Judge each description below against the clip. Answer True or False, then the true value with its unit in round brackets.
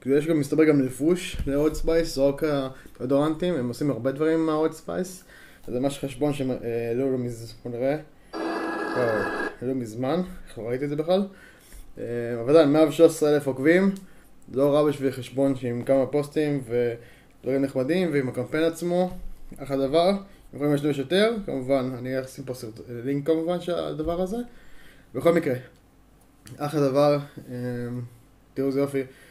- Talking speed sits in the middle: True (135 wpm)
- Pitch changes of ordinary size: True (3.7 semitones)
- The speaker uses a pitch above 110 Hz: True (140 Hz)